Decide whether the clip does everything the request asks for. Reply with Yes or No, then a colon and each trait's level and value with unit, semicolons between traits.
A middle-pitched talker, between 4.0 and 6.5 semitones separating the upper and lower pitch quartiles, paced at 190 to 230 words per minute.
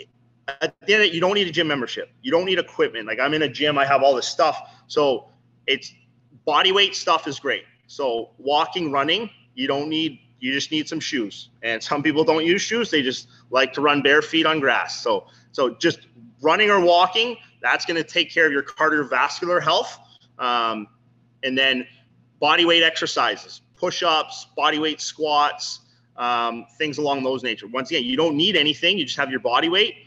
Yes: medium, 150 Hz; average, 4.8 semitones; average, 200 wpm